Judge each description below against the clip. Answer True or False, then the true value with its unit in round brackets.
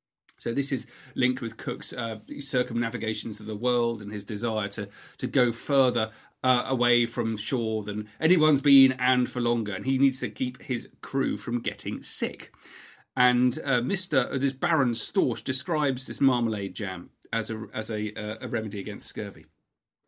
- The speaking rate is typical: True (175 wpm)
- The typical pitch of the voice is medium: False (120 Hz)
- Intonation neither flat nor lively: True (3.2 semitones)